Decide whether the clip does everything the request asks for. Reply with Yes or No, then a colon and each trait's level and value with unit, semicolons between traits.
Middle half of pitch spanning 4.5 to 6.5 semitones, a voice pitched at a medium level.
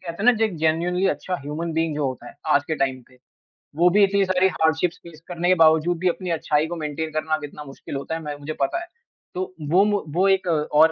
No: average, 3.0 semitones; medium, 160 Hz